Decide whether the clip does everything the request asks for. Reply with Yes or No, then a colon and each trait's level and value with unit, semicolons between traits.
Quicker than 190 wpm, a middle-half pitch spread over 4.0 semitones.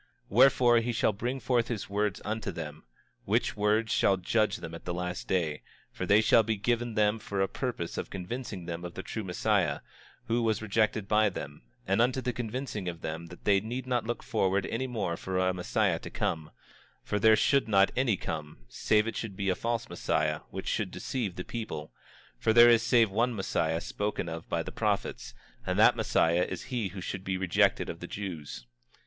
Yes: fast, 205 wpm; average, 4.4 semitones